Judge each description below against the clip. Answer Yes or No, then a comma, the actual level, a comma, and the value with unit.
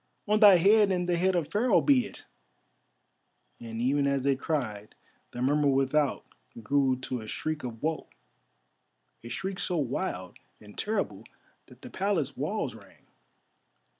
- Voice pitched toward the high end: No, medium, 145 Hz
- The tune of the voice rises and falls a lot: Yes, wide, 6.6 semitones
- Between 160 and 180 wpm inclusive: No, average, 150 wpm